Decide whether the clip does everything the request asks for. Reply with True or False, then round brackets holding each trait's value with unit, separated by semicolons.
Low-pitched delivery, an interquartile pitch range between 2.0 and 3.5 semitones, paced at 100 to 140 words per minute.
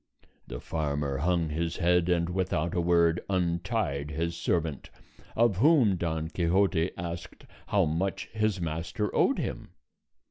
True (85 Hz; 2.5 semitones; 135 wpm)